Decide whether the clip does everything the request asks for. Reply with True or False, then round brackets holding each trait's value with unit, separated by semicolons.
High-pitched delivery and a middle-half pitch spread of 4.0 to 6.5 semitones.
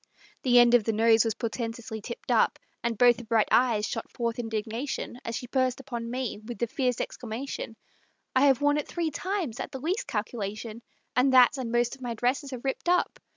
False (240 Hz; 2.7 semitones)